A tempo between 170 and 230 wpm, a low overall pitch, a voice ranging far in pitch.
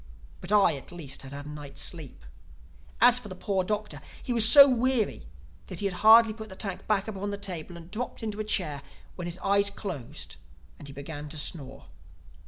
No: fast, 205 wpm; high, 190 Hz; wide, 6.3 semitones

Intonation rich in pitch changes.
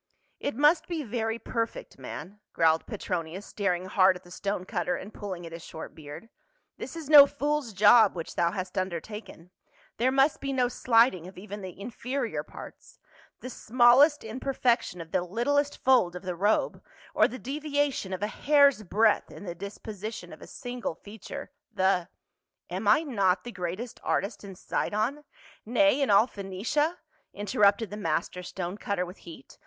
Yes: wide, 5.7 semitones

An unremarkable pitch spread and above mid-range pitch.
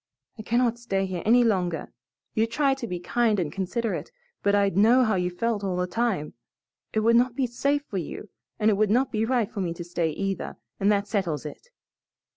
Yes: average, 4.3 semitones; high, 210 Hz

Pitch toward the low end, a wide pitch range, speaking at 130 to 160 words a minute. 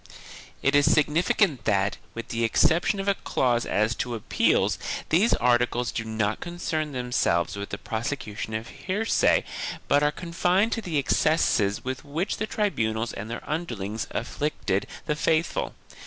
Yes: low, 130 Hz; wide, 6.8 semitones; average, 155 wpm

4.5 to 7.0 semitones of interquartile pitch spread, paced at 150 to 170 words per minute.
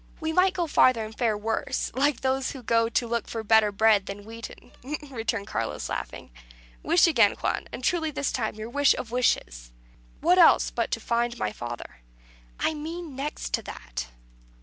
No: average, 5.0 semitones; average, 180 wpm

